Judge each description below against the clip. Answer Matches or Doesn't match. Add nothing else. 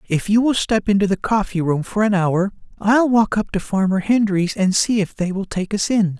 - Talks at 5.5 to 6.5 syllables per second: Doesn't match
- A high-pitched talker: Matches